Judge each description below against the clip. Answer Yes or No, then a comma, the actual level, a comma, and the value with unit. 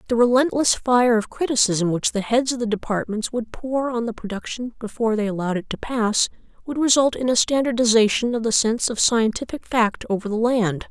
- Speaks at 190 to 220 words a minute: Yes, average, 200 wpm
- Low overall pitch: No, high, 230 Hz